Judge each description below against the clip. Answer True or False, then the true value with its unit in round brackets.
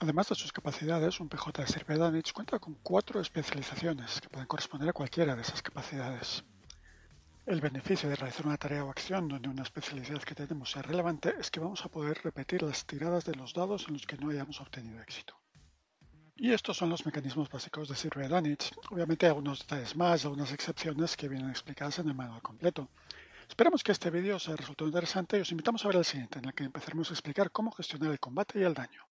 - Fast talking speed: True (215 wpm)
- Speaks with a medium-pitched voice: True (155 Hz)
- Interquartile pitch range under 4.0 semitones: True (3.5 semitones)